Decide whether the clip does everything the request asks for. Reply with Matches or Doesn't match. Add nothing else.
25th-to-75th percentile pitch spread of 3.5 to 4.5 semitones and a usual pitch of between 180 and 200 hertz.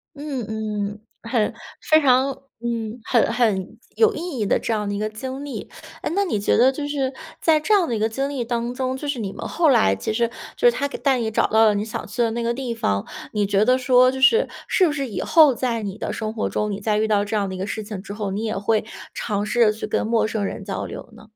Doesn't match